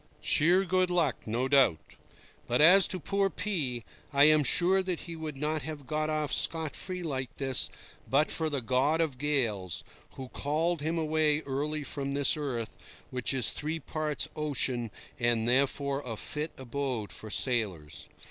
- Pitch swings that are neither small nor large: Yes, average, 3.6 semitones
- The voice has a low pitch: No, medium, 145 Hz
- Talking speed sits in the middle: Yes, average, 165 wpm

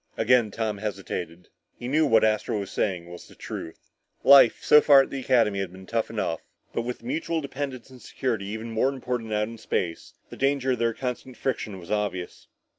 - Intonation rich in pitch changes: No, average, 4.5 semitones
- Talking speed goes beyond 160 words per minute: Yes, average, 195 wpm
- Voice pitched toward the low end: Yes, low, 115 Hz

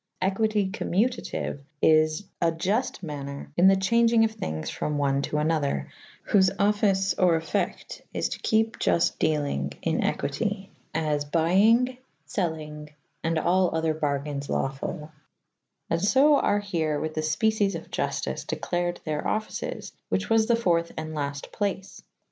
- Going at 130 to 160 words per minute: Yes, average, 155 wpm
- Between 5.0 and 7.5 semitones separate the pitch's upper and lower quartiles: Yes, average, 5.3 semitones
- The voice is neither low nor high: Yes, medium, 170 Hz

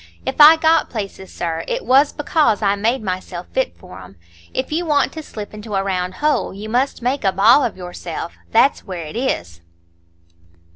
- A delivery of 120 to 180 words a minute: No, average, 190 wpm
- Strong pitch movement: Yes, wide, 6.6 semitones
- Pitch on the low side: No, high, 215 Hz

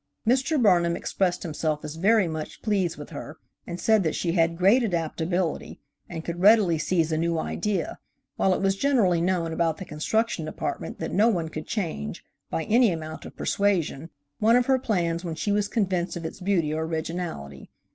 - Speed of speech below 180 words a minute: No, average, 185 wpm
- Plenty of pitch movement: No, average, 4.0 semitones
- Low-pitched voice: No, medium, 175 Hz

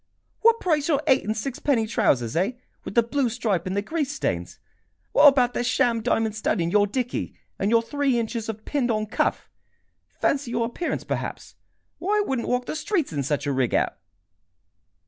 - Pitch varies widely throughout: No, average, 4.8 semitones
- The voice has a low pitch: No, high, 235 Hz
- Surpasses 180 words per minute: Yes, average, 190 wpm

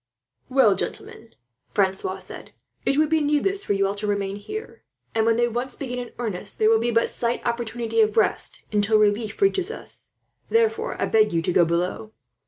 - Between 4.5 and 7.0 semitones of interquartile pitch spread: No, average, 3.8 semitones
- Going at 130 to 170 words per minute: No, average, 190 wpm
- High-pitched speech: Yes, high, 225 Hz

